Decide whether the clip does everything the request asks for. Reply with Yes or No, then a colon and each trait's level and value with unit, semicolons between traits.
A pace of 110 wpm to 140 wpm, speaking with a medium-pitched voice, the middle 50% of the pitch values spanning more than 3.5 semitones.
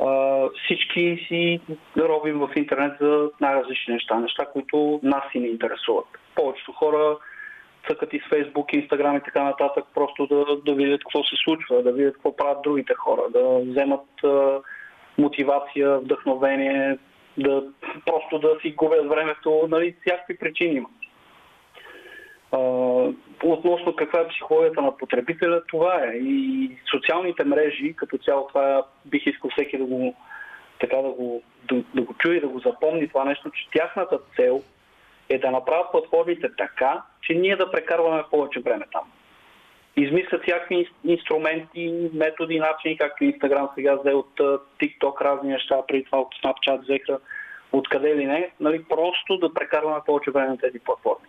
No: average, 150 wpm; medium, 150 Hz; average, 4.0 semitones